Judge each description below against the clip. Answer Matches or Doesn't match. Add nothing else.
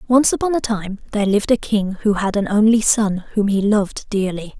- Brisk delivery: Matches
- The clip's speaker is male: Doesn't match